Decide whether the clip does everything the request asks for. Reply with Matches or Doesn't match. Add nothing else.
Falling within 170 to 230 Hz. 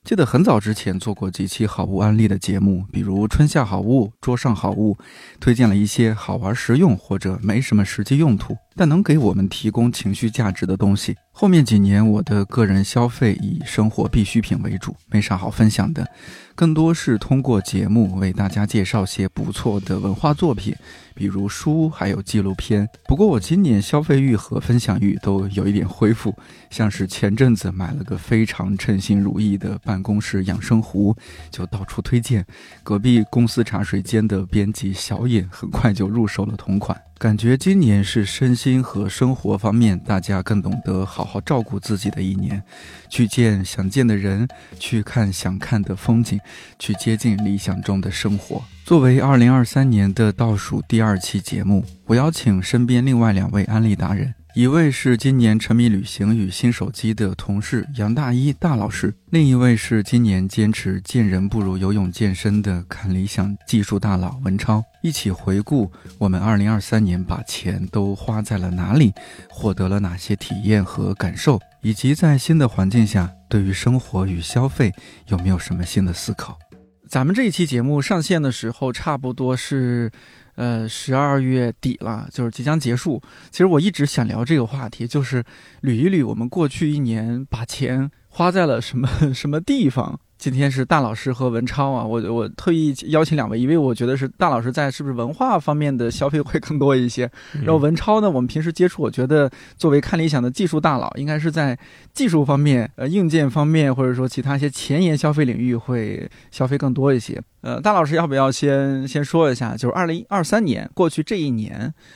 Doesn't match